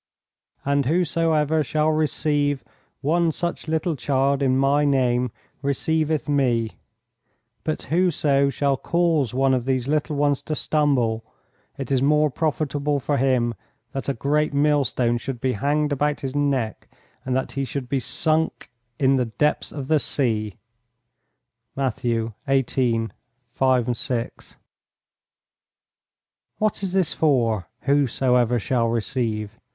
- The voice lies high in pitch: No, medium, 140 Hz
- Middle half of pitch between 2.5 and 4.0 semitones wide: Yes, average, 3.2 semitones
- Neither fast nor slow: No, slow, 125 wpm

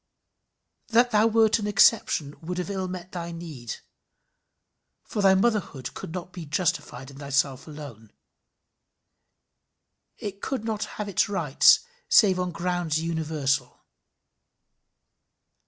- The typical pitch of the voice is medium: Yes, medium, 175 Hz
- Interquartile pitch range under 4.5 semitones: No, wide, 5.5 semitones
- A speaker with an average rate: No, slow, 120 wpm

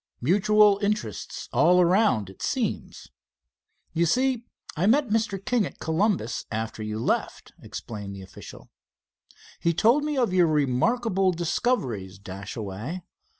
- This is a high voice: No, medium, 175 Hz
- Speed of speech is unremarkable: No, slow, 125 wpm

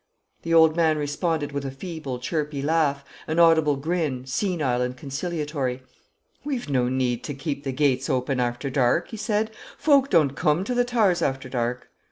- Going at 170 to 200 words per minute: Yes, average, 175 wpm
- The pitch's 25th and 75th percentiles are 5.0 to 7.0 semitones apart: No, average, 4.2 semitones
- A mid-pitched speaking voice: Yes, medium, 145 Hz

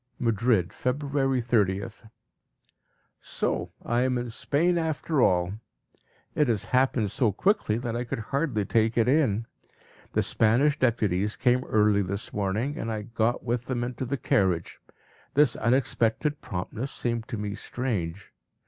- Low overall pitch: Yes, low, 115 Hz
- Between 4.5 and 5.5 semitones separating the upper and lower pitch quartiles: No, average, 3.6 semitones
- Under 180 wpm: Yes, average, 140 wpm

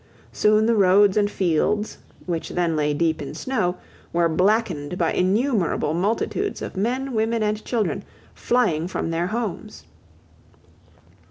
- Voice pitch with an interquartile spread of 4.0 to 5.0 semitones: Yes, average, 4.6 semitones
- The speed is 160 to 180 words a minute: No, slow, 135 wpm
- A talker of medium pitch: No, high, 200 Hz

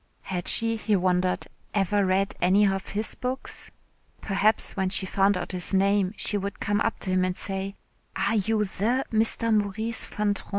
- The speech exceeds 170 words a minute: Yes, average, 180 wpm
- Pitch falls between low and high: No, high, 200 Hz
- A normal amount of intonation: No, narrow, 2.2 semitones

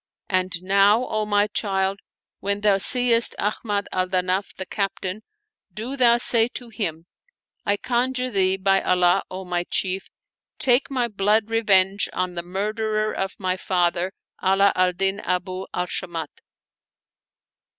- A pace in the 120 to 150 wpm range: Yes, average, 140 wpm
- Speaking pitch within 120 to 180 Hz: No, high, 195 Hz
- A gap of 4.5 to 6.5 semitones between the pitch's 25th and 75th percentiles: No, average, 2.7 semitones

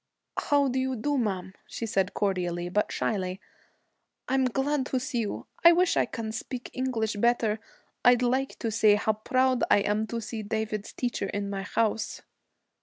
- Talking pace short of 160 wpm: No, average, 175 wpm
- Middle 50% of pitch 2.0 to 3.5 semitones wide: No, average, 3.9 semitones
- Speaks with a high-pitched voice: Yes, high, 225 Hz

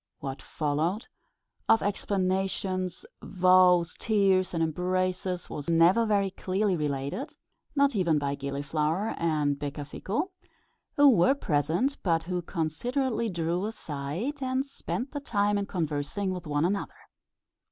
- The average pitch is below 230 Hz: Yes, medium, 185 Hz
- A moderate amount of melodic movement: Yes, average, 4.8 semitones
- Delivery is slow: Yes, slow, 120 wpm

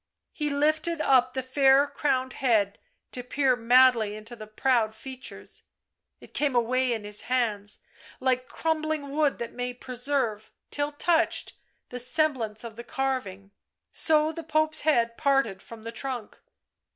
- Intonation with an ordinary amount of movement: Yes, average, 3.8 semitones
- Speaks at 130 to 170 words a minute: Yes, average, 145 wpm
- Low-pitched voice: No, very high, 255 Hz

